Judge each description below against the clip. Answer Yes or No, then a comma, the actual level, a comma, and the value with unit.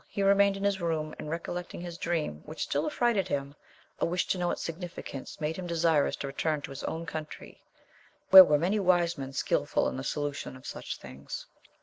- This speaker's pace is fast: Yes, fast, 210 wpm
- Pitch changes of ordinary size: Yes, average, 3.7 semitones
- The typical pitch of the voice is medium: Yes, medium, 165 Hz